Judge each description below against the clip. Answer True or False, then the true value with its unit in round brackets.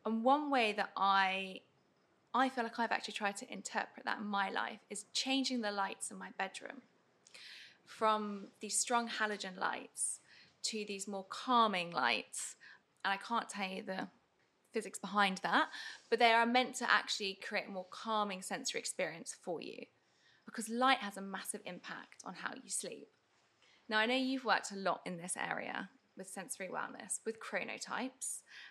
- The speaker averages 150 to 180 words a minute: True (170 wpm)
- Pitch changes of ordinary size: True (3.2 semitones)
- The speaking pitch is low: False (215 Hz)